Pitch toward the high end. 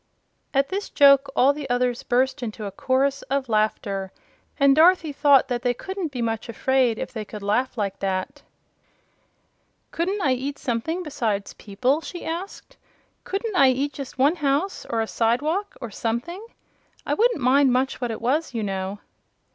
Yes: very high, 260 Hz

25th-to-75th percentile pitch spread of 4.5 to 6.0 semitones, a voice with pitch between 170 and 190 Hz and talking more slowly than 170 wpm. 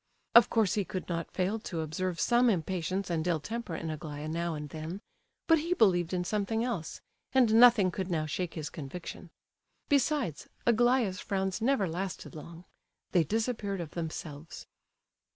Yes: wide, 5.4 semitones; medium, 185 Hz; average, 160 wpm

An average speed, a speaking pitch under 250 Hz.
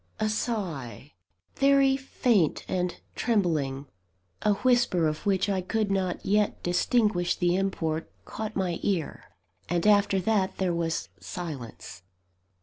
No: slow, 125 wpm; high, 190 Hz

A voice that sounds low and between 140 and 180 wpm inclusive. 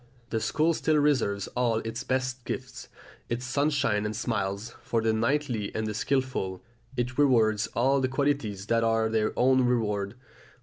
Yes: low, 120 Hz; average, 160 wpm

